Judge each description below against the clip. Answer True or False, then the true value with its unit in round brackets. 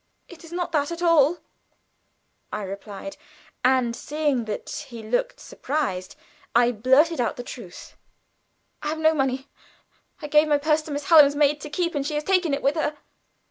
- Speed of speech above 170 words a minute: True (180 wpm)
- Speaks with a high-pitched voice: True (290 Hz)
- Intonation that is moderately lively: True (3.8 semitones)